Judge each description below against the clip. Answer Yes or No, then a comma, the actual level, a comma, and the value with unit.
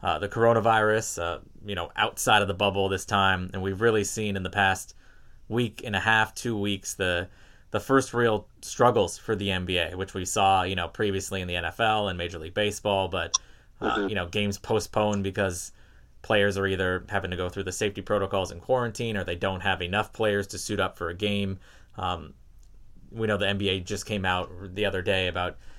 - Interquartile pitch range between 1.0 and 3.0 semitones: Yes, narrow, 2.4 semitones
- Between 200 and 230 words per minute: Yes, fast, 205 wpm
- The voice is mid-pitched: No, low, 100 Hz